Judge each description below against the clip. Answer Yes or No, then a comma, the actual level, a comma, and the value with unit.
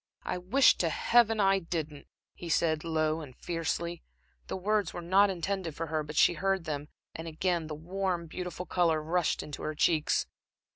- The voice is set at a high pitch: No, medium, 170 Hz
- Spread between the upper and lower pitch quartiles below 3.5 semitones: Yes, average, 3.0 semitones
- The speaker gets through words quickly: No, average, 180 wpm